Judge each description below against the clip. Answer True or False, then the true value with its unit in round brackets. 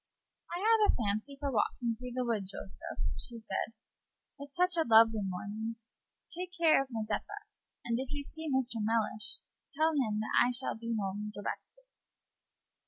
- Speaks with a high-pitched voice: True (235 Hz)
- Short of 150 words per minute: False (165 wpm)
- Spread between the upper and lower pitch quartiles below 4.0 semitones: False (4.9 semitones)